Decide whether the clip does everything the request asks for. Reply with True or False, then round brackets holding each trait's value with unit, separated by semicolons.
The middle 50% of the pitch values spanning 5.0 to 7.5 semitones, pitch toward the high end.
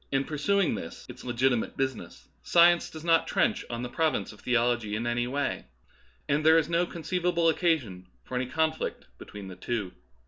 False (5.6 semitones; 135 Hz)